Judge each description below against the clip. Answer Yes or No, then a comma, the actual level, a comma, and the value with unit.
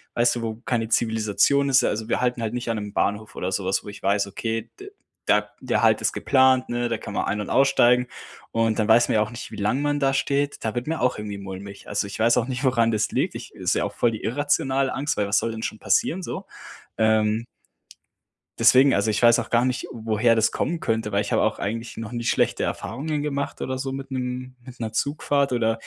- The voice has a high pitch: No, low, 115 Hz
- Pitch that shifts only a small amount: No, average, 3.3 semitones